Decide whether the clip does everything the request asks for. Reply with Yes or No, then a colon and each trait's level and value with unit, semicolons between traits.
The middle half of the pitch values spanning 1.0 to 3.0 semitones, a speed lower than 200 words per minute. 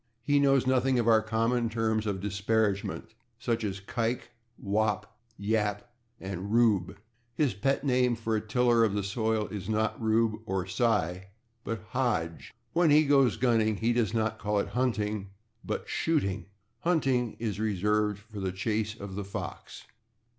Yes: average, 2.7 semitones; average, 155 wpm